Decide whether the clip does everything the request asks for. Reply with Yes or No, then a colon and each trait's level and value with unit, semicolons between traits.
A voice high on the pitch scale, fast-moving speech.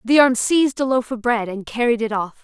Yes: high, 240 Hz; fast, 270 wpm